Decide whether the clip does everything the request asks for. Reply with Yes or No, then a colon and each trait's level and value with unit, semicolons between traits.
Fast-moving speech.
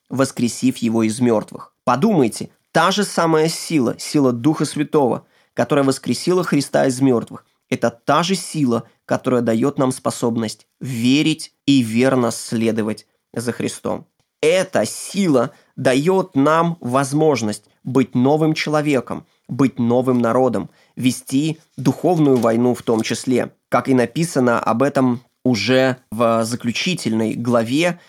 No: average, 120 wpm